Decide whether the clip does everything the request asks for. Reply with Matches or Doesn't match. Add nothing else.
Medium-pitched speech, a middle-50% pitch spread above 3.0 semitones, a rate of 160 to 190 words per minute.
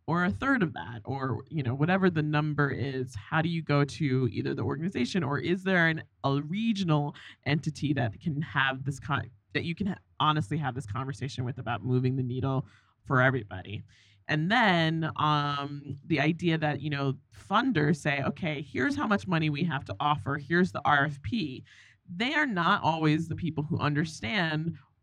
Matches